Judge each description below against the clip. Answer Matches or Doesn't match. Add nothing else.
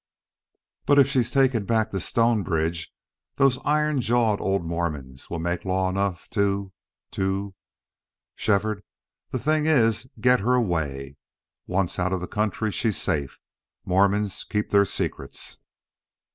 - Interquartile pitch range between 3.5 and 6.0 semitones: Matches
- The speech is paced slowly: Matches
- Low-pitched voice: Matches